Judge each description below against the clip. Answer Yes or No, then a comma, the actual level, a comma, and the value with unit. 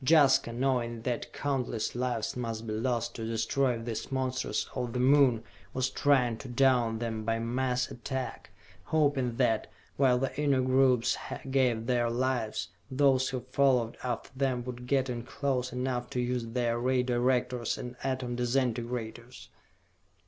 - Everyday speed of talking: Yes, average, 150 wpm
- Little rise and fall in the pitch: Yes, narrow, 1.8 semitones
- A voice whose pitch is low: Yes, low, 125 Hz